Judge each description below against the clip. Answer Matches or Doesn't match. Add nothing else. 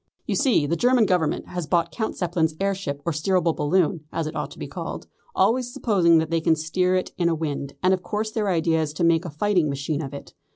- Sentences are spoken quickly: Matches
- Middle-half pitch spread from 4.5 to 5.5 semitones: Doesn't match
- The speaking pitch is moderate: Matches